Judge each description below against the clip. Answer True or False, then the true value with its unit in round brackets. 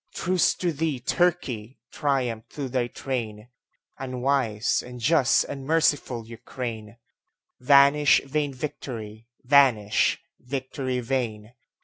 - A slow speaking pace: True (90 wpm)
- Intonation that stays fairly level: False (3.4 semitones)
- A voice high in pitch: False (130 Hz)